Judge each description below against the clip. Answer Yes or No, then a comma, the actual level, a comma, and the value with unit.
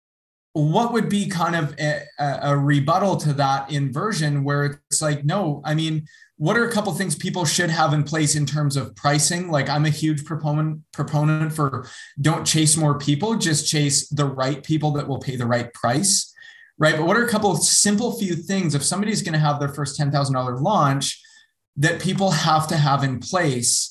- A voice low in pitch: No, medium, 155 Hz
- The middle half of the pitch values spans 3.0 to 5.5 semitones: Yes, average, 3.5 semitones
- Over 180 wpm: Yes, average, 200 wpm